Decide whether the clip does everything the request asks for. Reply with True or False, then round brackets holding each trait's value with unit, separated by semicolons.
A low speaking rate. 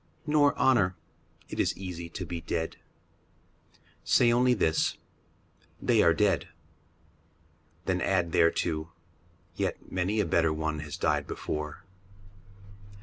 True (125 wpm)